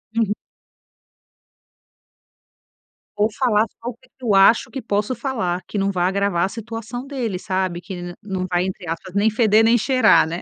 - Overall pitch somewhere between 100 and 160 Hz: No, high, 205 Hz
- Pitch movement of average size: Yes, average, 3.6 semitones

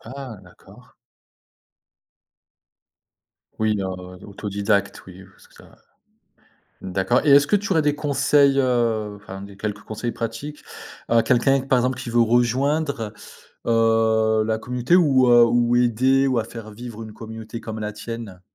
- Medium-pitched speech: No, low, 115 Hz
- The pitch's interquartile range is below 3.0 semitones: No, average, 3.3 semitones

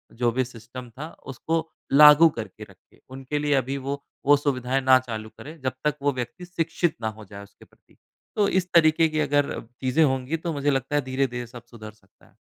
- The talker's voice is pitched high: No, low, 135 Hz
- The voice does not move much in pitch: No, average, 3.7 semitones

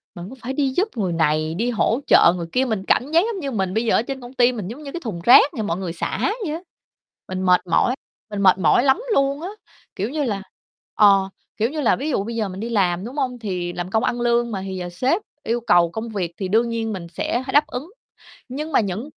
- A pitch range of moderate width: No, wide, 5.8 semitones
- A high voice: Yes, high, 225 Hz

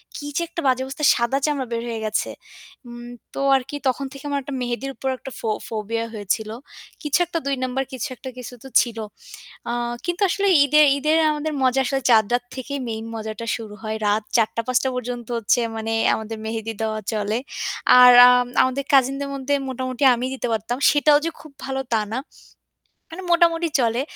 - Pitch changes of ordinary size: Yes, average, 3.6 semitones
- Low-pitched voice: No, very high, 250 Hz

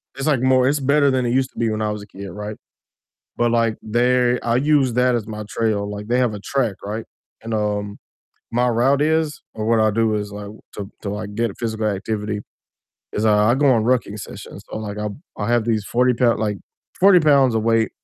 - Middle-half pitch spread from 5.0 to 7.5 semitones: No, average, 3.2 semitones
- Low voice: Yes, low, 115 Hz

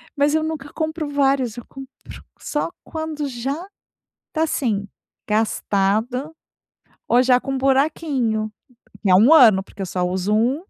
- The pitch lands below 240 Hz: No, very high, 265 Hz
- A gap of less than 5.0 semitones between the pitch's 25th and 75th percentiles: No, wide, 5.4 semitones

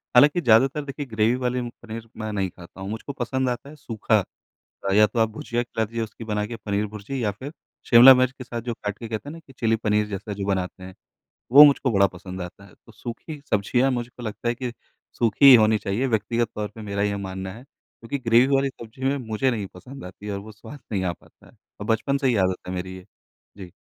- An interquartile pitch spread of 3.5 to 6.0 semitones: Yes, average, 3.8 semitones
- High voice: No, low, 110 Hz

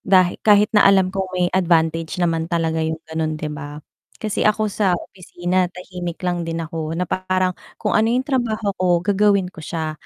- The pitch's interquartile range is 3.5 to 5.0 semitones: No, average, 3.1 semitones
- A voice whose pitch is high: No, medium, 180 Hz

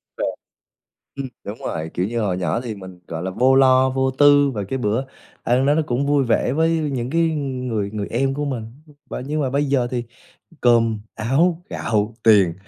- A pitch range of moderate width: Yes, average, 4.2 semitones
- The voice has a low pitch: Yes, low, 125 Hz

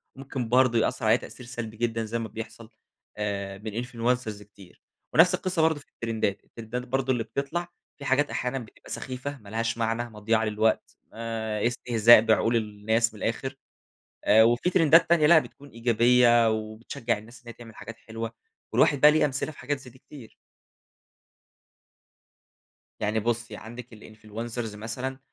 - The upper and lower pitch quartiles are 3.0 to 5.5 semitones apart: No, narrow, 2.6 semitones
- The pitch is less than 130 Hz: Yes, low, 115 Hz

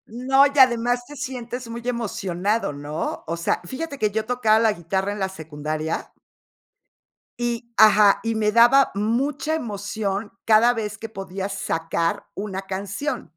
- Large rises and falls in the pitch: No, average, 4.0 semitones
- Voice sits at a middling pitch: No, high, 215 Hz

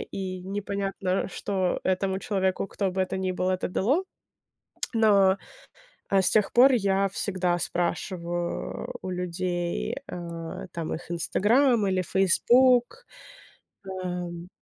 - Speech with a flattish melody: Yes, narrow, 1.9 semitones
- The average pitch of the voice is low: No, high, 190 Hz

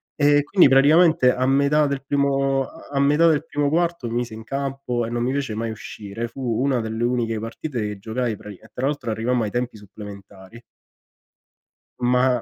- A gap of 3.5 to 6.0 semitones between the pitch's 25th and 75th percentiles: Yes, average, 3.8 semitones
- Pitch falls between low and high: No, low, 125 Hz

